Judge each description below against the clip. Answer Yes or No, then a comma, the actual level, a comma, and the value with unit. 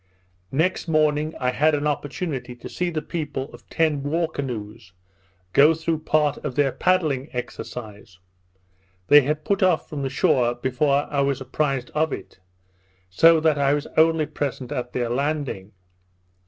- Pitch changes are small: No, average, 3.4 semitones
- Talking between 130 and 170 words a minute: Yes, average, 155 wpm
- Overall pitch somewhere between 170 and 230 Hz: No, medium, 145 Hz